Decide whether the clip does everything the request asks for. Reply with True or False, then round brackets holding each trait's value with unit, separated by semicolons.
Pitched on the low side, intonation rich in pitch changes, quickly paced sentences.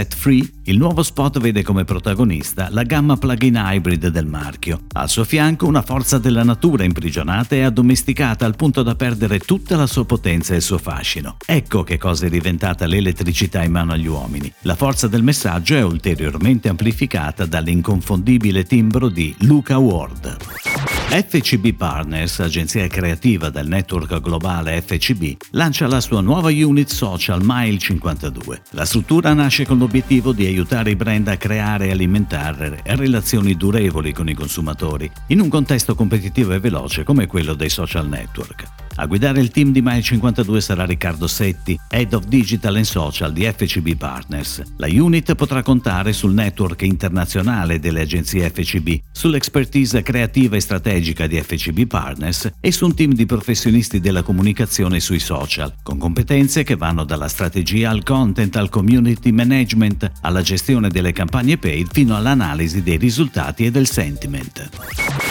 False (100 Hz; 6.5 semitones; 155 wpm)